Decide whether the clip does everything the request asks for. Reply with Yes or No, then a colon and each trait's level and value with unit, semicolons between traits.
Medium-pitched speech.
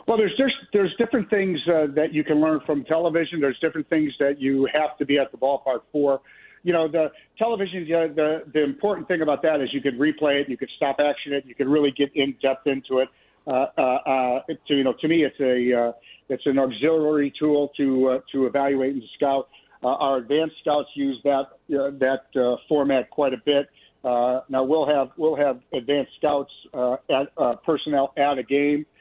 Yes: medium, 145 Hz